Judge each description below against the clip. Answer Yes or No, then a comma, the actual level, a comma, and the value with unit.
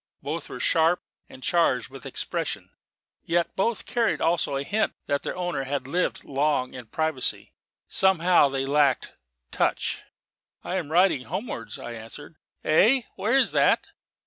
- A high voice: No, medium, 160 Hz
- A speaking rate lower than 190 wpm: Yes, average, 145 wpm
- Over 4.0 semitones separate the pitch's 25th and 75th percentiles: Yes, average, 5.0 semitones